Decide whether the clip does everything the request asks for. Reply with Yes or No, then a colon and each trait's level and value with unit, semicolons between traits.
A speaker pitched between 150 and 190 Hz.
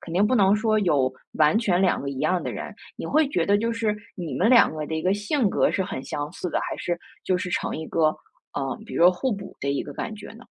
Yes: medium, 185 Hz